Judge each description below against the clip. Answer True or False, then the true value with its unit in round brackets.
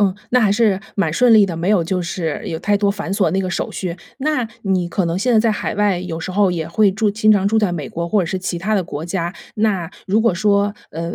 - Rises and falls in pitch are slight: False (3.3 semitones)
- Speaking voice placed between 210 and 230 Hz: False (195 Hz)